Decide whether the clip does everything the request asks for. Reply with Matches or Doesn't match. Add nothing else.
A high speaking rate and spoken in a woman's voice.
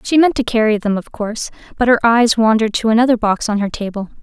Matches